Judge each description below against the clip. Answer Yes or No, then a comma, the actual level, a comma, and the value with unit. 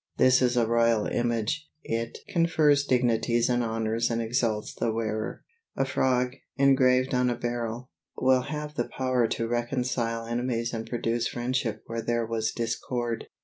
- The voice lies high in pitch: No, low, 120 Hz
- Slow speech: No, average, 150 wpm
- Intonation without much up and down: Yes, narrow, 1.8 semitones